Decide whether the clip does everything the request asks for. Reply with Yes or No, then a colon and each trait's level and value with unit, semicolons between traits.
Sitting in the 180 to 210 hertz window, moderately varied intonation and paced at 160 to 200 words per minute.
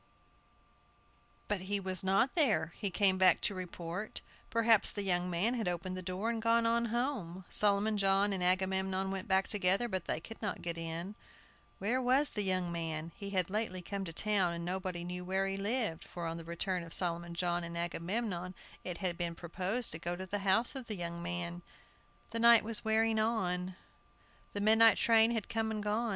Yes: high, 190 Hz; average, 3.8 semitones; average, 195 wpm